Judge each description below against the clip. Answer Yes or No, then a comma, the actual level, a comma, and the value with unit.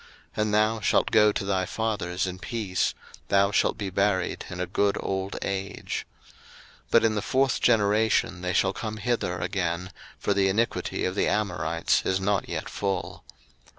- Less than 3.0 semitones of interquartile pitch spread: Yes, narrow, 2.6 semitones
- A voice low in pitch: Yes, low, 100 Hz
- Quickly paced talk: No, average, 175 wpm